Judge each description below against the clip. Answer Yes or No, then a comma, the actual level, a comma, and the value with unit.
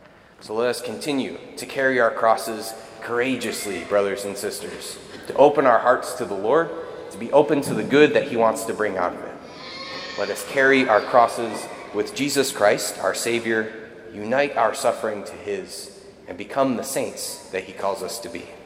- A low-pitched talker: Yes, low, 120 Hz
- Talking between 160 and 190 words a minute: Yes, average, 185 wpm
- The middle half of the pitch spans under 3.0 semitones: No, average, 4.4 semitones